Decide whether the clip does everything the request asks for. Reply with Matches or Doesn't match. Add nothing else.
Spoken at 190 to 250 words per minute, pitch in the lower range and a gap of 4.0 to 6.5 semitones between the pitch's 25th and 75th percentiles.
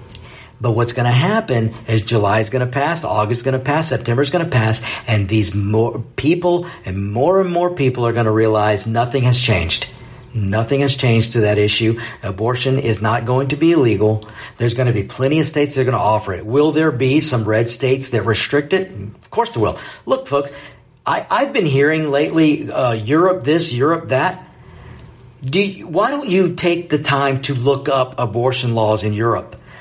Matches